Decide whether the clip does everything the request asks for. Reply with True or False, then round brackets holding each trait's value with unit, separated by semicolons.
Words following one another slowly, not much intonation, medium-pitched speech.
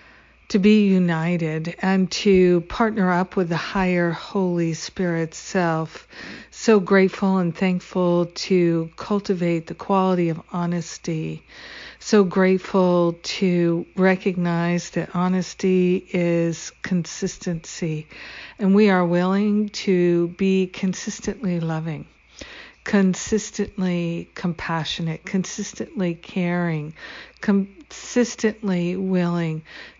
True (90 wpm; 2.3 semitones; 180 Hz)